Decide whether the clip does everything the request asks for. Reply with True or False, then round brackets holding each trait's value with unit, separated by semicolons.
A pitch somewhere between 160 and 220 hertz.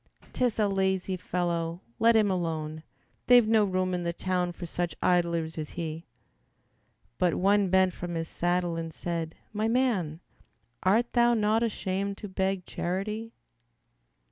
True (185 Hz)